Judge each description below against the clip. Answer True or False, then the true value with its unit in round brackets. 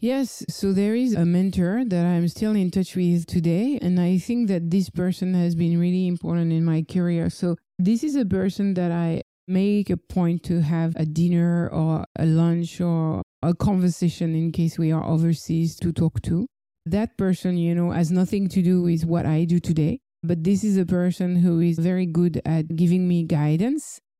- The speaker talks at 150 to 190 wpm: False (200 wpm)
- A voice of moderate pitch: True (175 Hz)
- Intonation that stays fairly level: True (1.9 semitones)